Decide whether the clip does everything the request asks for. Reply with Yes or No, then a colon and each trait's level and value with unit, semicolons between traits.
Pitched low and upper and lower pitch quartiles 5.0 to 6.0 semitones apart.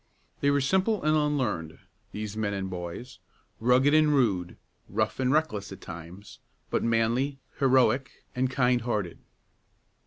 Yes: low, 125 Hz; average, 5.3 semitones